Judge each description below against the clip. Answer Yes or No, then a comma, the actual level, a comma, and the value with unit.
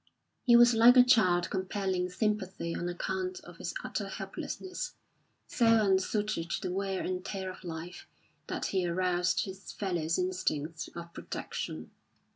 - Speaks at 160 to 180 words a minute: No, average, 145 wpm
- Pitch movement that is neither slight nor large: Yes, average, 3.2 semitones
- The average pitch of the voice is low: No, medium, 185 Hz